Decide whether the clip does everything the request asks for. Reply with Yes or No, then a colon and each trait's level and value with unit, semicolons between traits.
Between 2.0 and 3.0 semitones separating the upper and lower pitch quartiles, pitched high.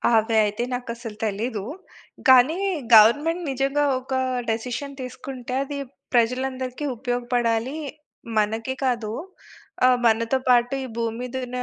Yes: narrow, 2.5 semitones; high, 245 Hz